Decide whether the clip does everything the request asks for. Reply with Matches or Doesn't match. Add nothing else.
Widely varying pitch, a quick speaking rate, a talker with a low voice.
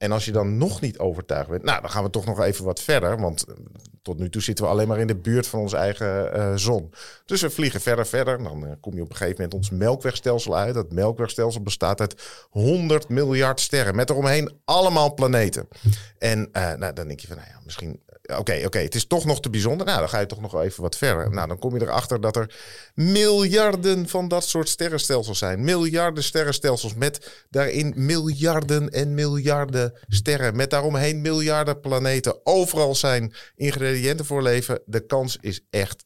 Matches